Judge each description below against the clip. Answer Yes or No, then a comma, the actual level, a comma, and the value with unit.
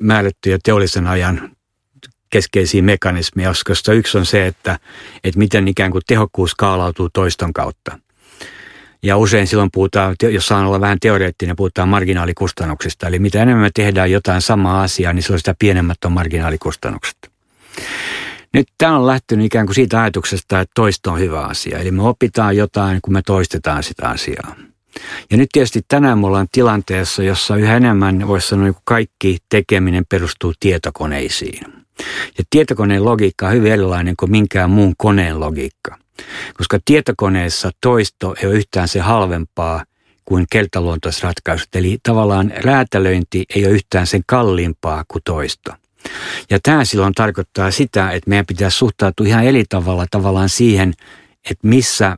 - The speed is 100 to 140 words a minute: No, average, 150 wpm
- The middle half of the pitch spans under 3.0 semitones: Yes, narrow, 2.6 semitones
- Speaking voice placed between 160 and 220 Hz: No, very low, 95 Hz